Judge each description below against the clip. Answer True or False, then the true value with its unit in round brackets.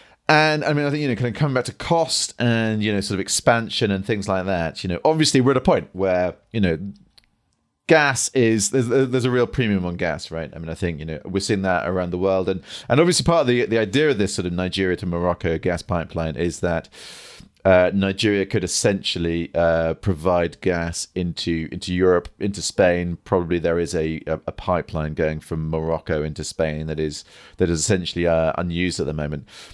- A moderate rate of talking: False (220 wpm)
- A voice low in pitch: True (90 Hz)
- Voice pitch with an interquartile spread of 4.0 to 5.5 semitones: True (4.9 semitones)